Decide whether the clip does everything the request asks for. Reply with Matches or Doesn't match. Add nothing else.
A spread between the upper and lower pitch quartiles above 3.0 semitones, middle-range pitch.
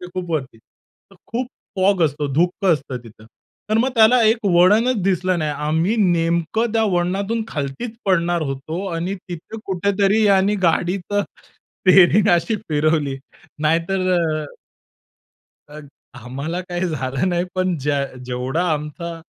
Matches